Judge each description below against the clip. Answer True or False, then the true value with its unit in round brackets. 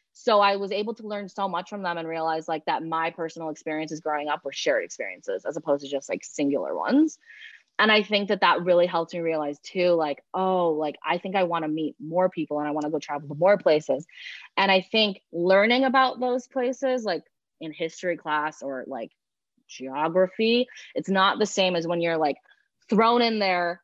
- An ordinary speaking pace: False (210 wpm)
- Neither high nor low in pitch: True (175 Hz)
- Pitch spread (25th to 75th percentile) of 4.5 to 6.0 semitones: True (4.9 semitones)